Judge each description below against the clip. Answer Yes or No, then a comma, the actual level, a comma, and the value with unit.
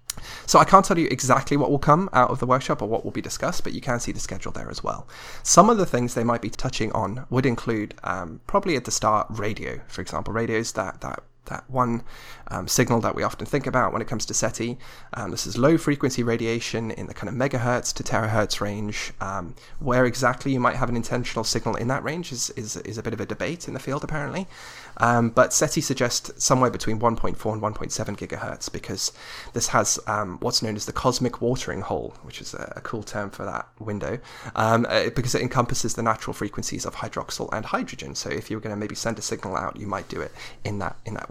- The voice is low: Yes, low, 120 Hz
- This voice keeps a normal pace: No, fast, 230 wpm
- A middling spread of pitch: Yes, average, 3.0 semitones